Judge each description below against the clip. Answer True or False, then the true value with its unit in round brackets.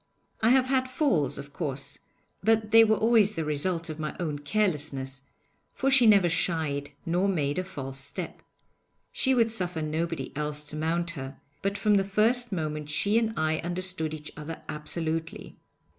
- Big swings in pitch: True (5.8 semitones)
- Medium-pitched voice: True (170 Hz)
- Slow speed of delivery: False (170 wpm)